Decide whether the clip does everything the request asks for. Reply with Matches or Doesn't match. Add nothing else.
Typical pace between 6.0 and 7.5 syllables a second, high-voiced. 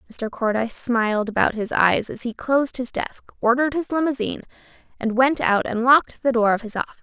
Matches